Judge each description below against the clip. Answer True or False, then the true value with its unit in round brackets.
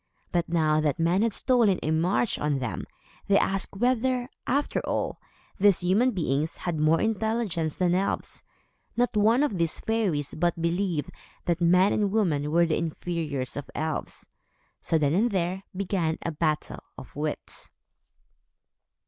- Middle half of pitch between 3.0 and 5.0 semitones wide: True (4.7 semitones)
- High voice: False (175 Hz)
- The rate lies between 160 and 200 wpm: False (150 wpm)